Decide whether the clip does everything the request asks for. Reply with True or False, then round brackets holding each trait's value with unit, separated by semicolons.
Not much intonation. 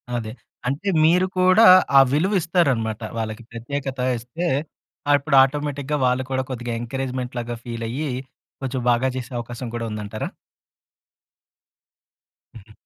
False (3.7 semitones)